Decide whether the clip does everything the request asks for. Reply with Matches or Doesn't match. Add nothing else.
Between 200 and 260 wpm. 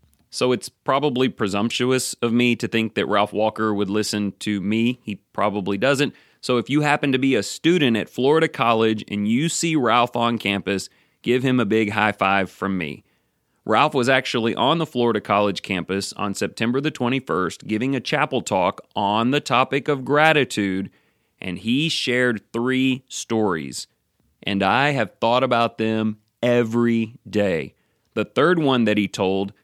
Doesn't match